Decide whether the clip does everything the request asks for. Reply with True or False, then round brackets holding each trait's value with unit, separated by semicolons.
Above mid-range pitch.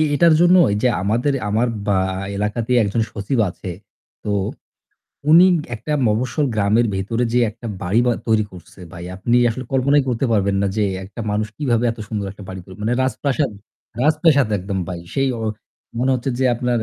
False (115 Hz)